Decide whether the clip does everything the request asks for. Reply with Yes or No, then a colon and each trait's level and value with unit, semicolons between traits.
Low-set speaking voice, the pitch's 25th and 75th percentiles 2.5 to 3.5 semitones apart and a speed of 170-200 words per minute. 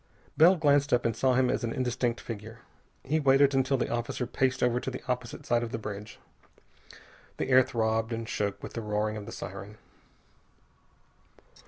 Yes: low, 120 Hz; average, 2.8 semitones; average, 180 wpm